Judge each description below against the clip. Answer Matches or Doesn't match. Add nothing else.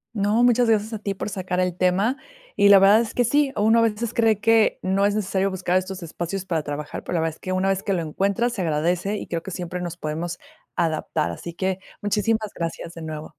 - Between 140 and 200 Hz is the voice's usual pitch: Matches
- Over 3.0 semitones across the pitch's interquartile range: Matches